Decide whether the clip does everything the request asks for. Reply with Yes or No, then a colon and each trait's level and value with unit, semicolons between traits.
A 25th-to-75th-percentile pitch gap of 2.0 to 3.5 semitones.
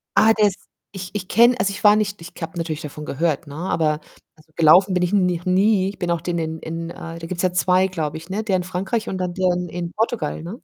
Yes: average, 2.7 semitones